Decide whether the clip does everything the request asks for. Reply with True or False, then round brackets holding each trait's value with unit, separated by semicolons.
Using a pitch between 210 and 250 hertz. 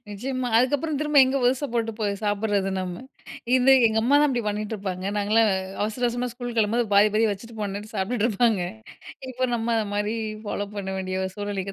True (220 Hz)